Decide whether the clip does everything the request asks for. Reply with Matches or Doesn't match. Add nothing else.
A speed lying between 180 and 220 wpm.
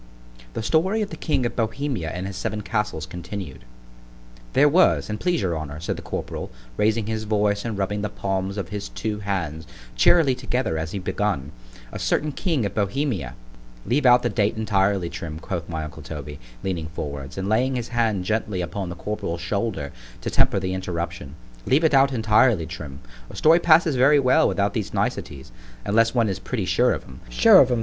Matches